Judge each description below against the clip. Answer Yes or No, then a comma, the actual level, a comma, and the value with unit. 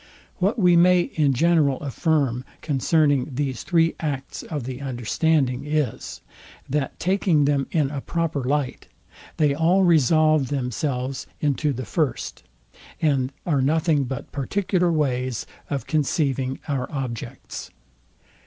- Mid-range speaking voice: Yes, medium, 145 Hz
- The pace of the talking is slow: Yes, slow, 125 wpm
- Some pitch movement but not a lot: Yes, average, 3.4 semitones